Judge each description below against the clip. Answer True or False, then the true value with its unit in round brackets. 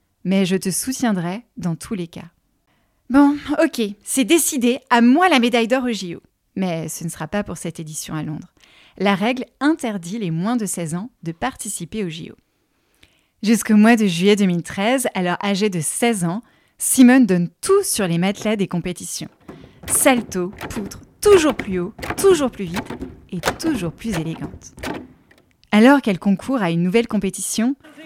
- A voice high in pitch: True (210 Hz)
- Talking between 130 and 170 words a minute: True (165 wpm)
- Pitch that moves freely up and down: True (6.0 semitones)